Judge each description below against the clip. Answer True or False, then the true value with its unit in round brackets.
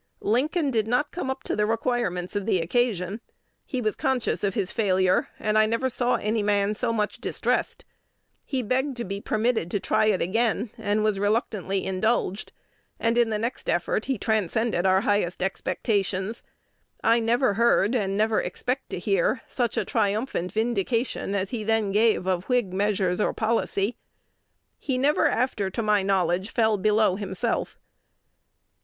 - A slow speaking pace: False (165 wpm)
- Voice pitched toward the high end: True (215 Hz)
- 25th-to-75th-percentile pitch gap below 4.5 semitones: True (3.4 semitones)